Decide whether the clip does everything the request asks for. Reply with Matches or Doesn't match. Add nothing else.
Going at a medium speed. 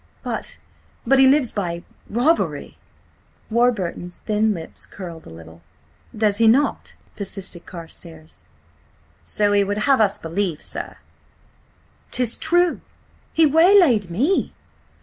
Doesn't match